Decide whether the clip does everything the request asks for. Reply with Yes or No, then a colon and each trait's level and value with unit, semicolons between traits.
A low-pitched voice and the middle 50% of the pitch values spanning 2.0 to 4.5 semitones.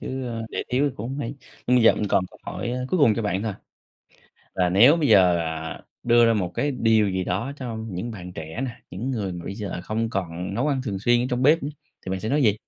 No: low, 110 Hz; average, 5.1 semitones